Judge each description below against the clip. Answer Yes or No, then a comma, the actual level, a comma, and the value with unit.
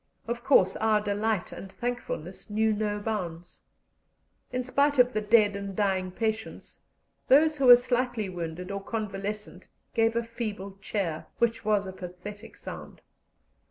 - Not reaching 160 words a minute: Yes, average, 145 wpm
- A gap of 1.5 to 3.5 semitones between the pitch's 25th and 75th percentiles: Yes, average, 3.2 semitones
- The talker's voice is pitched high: Yes, high, 210 Hz